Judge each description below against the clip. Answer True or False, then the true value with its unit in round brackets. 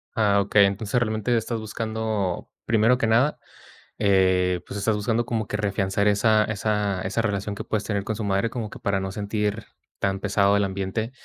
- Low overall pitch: True (105 Hz)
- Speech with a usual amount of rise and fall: False (2.0 semitones)